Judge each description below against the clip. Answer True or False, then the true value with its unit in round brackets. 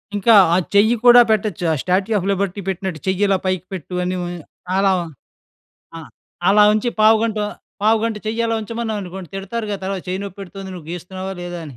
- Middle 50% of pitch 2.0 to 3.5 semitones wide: True (2.8 semitones)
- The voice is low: False (195 Hz)